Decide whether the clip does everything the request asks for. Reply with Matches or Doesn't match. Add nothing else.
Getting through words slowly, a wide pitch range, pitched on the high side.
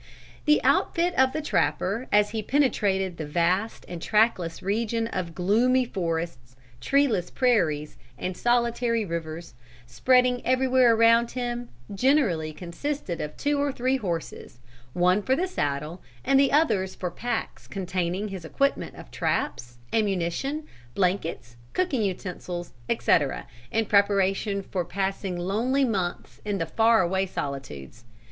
Matches